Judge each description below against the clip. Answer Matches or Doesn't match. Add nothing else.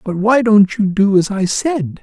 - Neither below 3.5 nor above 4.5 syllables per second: Matches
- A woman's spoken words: Doesn't match